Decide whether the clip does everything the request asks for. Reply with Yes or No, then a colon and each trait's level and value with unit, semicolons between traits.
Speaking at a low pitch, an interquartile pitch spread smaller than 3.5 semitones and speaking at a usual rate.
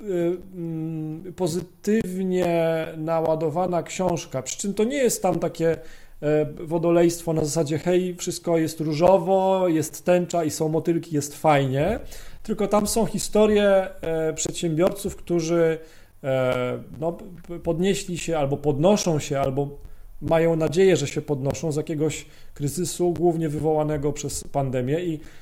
No: medium, 165 Hz; narrow, 2.5 semitones; average, 120 wpm